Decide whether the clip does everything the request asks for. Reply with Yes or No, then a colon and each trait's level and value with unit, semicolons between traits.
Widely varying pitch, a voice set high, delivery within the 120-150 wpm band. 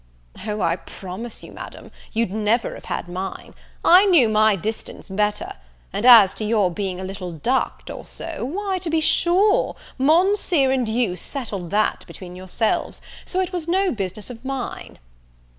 No: wide, 8.4 semitones; high, 225 Hz; average, 165 wpm